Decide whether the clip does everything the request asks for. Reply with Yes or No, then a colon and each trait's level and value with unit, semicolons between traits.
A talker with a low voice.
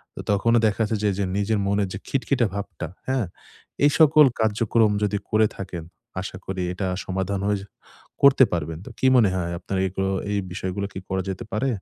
Yes: low, 100 Hz